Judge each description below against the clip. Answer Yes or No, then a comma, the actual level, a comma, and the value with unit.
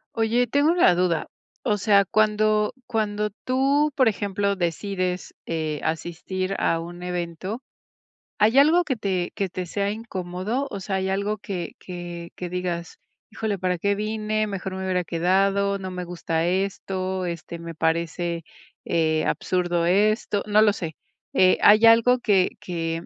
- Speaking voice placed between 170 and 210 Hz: Yes, high, 190 Hz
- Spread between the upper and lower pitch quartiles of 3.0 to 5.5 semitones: Yes, average, 3.4 semitones